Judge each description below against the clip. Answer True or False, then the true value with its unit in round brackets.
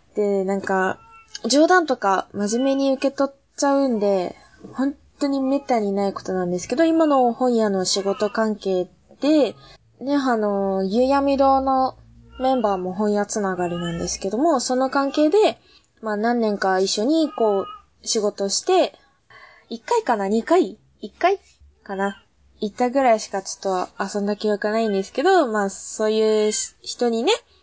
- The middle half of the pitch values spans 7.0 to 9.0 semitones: False (5.7 semitones)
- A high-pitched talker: True (220 Hz)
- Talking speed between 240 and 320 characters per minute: True (295 characters per minute)